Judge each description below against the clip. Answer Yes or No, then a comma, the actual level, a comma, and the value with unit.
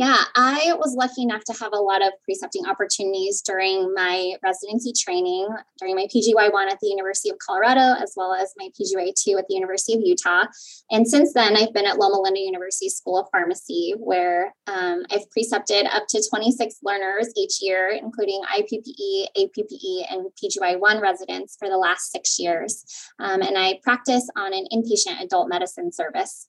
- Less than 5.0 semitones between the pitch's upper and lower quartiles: No, wide, 5.5 semitones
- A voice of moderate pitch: No, high, 215 Hz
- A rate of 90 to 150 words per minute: No, average, 175 wpm